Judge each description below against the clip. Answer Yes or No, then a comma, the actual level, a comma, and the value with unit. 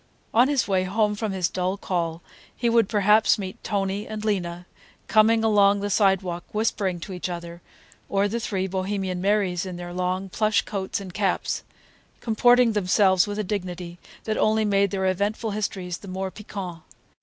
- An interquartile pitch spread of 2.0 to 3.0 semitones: Yes, narrow, 2.6 semitones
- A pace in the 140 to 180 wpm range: Yes, average, 170 wpm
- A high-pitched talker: Yes, high, 195 Hz